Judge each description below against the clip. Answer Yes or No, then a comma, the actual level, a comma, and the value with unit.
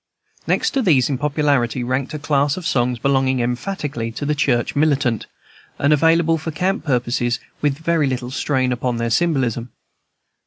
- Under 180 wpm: Yes, average, 160 wpm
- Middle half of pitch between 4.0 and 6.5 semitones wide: No, average, 3.6 semitones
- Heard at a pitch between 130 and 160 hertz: Yes, medium, 140 Hz